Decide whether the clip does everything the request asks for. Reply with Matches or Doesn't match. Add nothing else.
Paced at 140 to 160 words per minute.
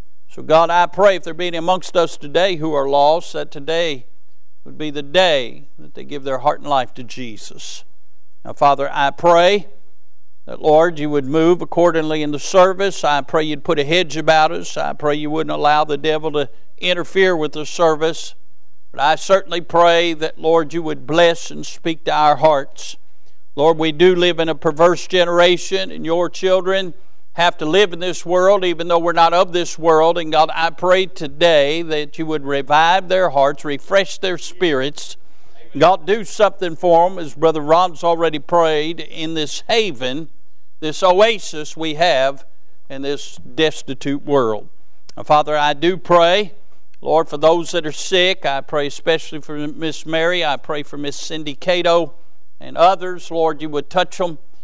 Doesn't match